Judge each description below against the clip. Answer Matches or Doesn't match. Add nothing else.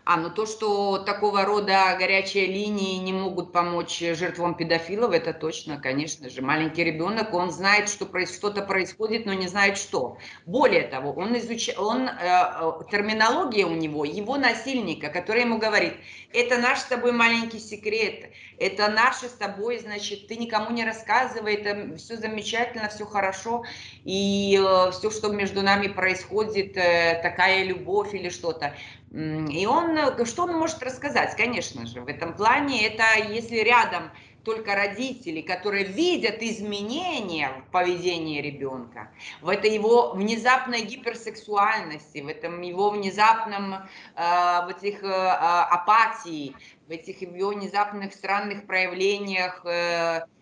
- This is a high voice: Matches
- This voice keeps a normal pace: Matches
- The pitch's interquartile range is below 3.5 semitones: Doesn't match